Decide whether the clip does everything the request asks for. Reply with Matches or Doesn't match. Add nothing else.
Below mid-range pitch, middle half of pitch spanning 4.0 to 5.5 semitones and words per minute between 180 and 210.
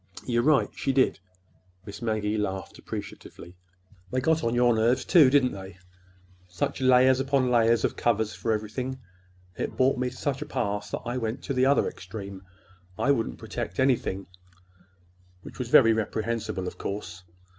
Doesn't match